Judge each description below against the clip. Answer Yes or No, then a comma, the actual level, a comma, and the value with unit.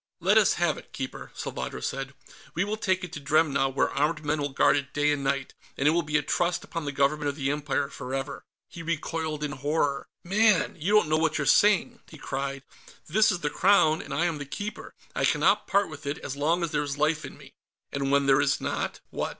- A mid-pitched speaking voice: Yes, medium, 150 Hz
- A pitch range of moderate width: Yes, average, 3.1 semitones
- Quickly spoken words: Yes, fast, 235 wpm